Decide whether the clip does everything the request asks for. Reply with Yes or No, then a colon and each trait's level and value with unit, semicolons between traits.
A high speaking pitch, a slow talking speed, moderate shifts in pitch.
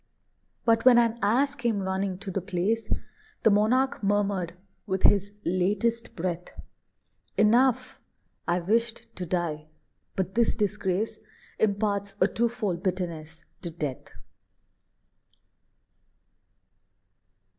Yes: high, 200 Hz; slow, 100 wpm; average, 3.8 semitones